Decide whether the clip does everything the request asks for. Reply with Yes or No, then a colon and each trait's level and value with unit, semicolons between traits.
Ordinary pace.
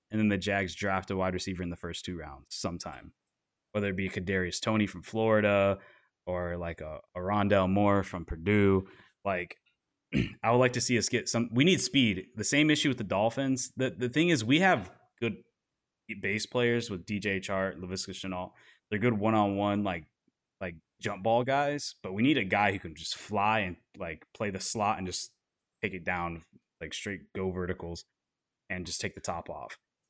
Yes: average, 195 wpm